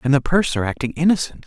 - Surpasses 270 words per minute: No, fast, 205 wpm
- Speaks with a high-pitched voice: No, medium, 145 Hz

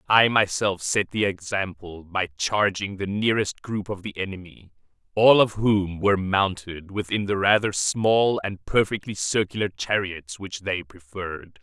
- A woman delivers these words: No, male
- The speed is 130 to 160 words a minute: Yes, average, 150 wpm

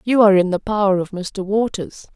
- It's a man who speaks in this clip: No, female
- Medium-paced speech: No, fast, 225 wpm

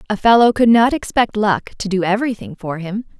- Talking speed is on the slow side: No, fast, 205 wpm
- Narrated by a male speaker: No, female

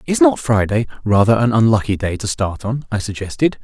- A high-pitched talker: No, low, 110 Hz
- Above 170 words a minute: Yes, average, 200 wpm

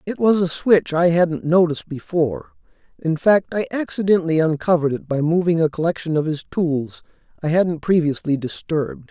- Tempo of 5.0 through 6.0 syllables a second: Yes, 5.4 syllables/s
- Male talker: Yes, male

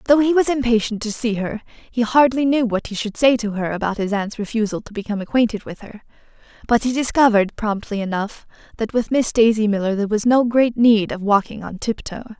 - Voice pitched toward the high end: Yes, high, 225 Hz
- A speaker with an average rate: No, fast, 215 wpm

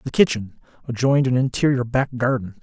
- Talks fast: No, average, 160 wpm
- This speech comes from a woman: No, male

